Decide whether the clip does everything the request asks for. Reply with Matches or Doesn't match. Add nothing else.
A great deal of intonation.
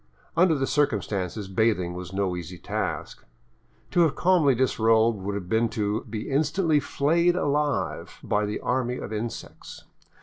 Matches